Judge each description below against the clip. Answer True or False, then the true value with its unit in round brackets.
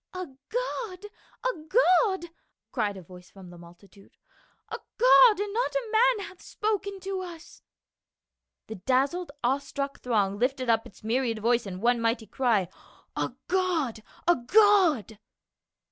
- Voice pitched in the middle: False (280 Hz)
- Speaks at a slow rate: False (160 wpm)